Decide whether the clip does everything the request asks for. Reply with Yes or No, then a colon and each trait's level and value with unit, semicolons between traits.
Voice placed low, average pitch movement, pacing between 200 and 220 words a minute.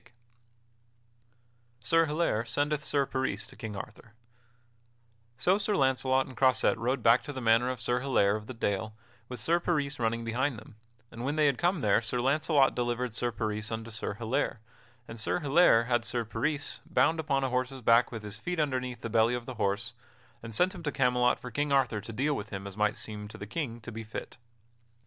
Yes: low, 125 Hz; average, 3.8 semitones; fast, 205 wpm